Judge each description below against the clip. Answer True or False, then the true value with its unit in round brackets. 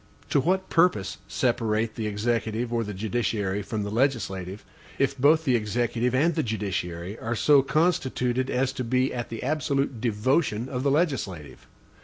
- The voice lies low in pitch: True (120 Hz)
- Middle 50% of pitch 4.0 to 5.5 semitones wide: True (4.3 semitones)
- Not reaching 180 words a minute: True (160 wpm)